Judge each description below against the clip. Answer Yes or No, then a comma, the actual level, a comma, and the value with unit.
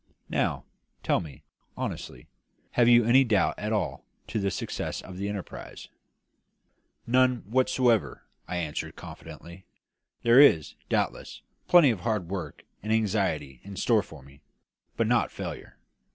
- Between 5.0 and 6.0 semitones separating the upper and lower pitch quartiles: Yes, wide, 5.4 semitones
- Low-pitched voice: Yes, low, 105 Hz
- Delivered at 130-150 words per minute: Yes, average, 140 wpm